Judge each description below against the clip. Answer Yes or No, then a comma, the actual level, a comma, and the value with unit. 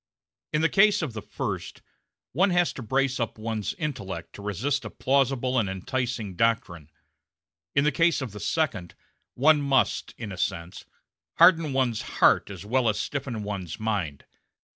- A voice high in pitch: No, low, 120 Hz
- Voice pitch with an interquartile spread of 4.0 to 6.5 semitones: Yes, wide, 5.4 semitones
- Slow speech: No, average, 165 wpm